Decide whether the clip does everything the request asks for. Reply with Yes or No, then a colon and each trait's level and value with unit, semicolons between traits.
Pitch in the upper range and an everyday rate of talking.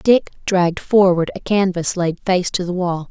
No: medium, 180 Hz; average, 195 wpm